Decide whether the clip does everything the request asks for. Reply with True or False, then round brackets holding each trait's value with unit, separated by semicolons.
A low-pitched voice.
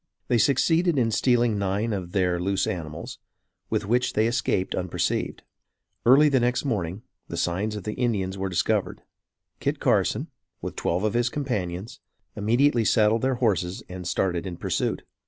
True (105 Hz)